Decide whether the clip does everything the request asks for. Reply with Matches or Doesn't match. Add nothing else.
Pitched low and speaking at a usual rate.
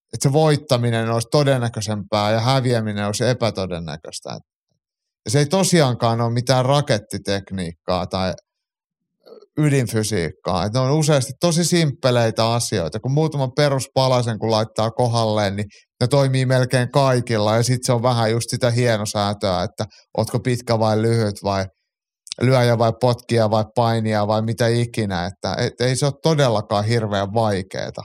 Matches